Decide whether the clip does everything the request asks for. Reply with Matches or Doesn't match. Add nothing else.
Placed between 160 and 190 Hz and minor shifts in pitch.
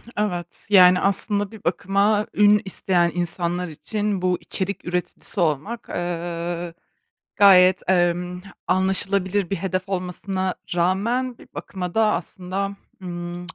Matches